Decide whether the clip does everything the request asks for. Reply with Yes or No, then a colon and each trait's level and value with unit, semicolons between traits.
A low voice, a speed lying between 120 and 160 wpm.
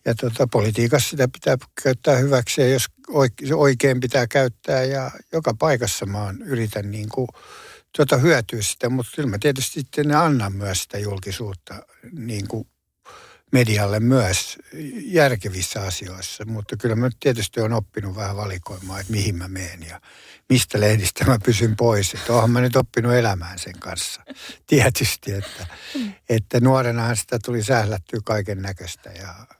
Yes: low, 115 Hz; fast, 155 wpm